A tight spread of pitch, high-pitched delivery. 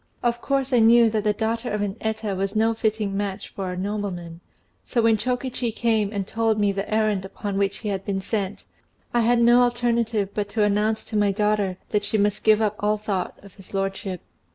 Yes: narrow, 2.2 semitones; high, 210 Hz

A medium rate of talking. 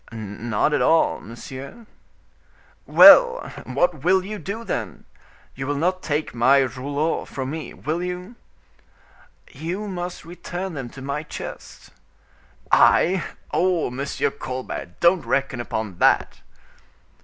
No: slow, 120 wpm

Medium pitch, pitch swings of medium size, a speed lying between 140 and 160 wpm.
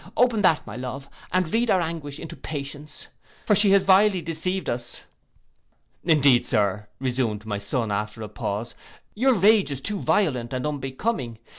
No: medium, 145 Hz; wide, 7.9 semitones; average, 155 wpm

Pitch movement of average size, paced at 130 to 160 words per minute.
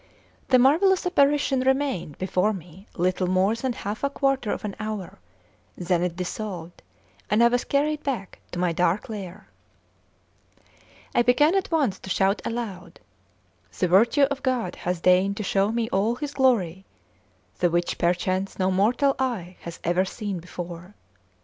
No: wide, 6.0 semitones; average, 155 wpm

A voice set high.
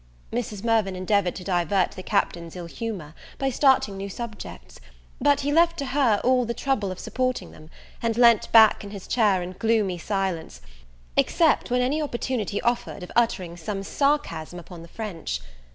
Yes: high, 210 Hz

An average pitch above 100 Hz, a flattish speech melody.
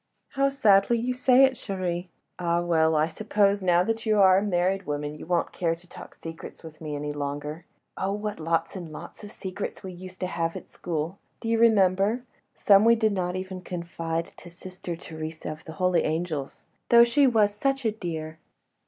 No: medium, 185 Hz; average, 4.2 semitones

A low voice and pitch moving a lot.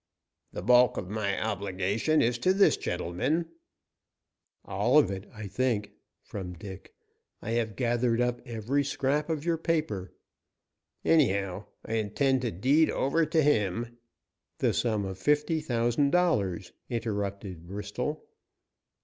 Yes: low, 115 Hz; wide, 6.0 semitones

